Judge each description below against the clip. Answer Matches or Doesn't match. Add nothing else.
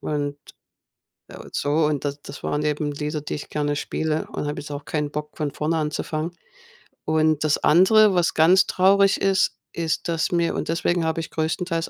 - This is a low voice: Doesn't match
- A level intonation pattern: Matches